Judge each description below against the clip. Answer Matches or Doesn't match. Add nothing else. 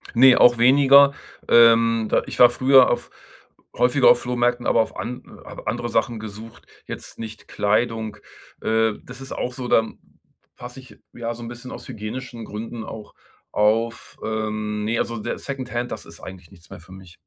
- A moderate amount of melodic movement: Doesn't match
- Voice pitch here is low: Matches